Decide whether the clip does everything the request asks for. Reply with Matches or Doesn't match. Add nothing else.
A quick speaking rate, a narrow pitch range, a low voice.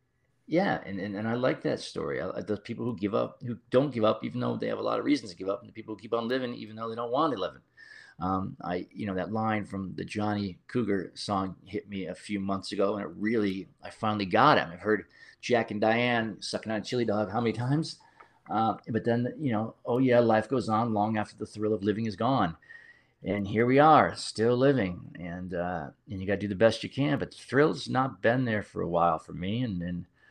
Doesn't match